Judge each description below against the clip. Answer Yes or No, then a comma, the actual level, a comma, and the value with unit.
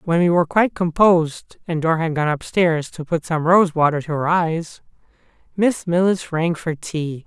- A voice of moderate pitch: Yes, medium, 165 Hz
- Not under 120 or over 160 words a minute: No, average, 200 wpm